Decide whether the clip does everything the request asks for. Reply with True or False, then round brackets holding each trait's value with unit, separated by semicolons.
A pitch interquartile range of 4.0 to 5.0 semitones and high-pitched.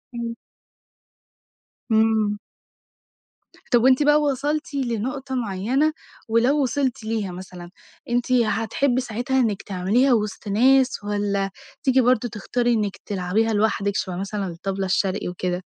True (4.3 semitones; 225 Hz)